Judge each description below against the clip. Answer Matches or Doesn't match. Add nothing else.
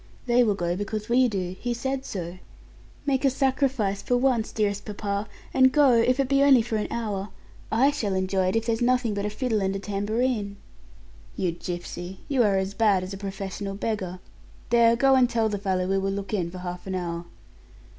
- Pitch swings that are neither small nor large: Matches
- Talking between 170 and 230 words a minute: Matches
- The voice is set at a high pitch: Matches